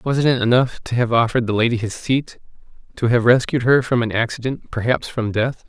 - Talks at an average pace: No, fast, 210 wpm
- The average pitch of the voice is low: Yes, low, 120 Hz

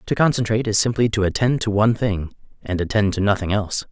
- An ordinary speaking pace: No, fast, 215 wpm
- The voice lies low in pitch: Yes, low, 105 Hz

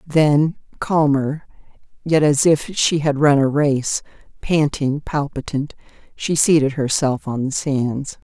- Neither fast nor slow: No, slow, 130 wpm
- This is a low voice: No, medium, 145 Hz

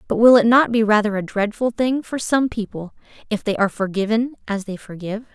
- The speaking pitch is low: No, high, 220 Hz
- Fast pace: Yes, fast, 215 wpm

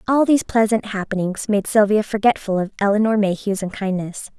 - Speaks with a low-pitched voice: No, high, 205 Hz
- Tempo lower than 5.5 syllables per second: No, 5.7 syllables/s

